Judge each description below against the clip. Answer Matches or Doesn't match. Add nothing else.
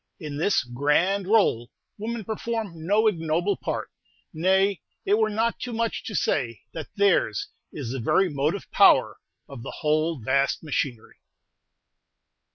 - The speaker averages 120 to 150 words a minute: Matches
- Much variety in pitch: Matches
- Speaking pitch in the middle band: Matches